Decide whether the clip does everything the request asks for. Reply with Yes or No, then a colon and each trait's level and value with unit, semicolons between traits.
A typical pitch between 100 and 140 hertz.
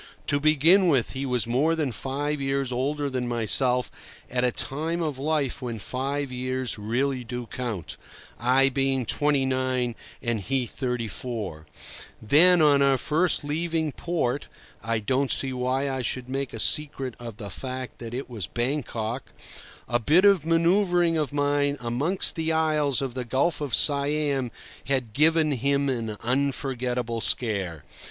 Yes: low, 135 Hz